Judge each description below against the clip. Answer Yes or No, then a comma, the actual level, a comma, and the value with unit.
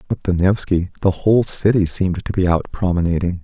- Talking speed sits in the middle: Yes, average, 190 wpm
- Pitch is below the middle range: Yes, very low, 90 Hz